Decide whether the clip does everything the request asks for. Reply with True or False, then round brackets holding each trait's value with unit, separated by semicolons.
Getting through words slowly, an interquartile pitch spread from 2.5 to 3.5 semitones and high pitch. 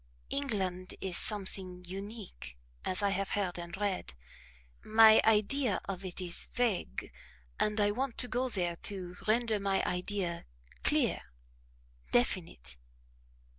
True (125 wpm; 3.2 semitones; 195 Hz)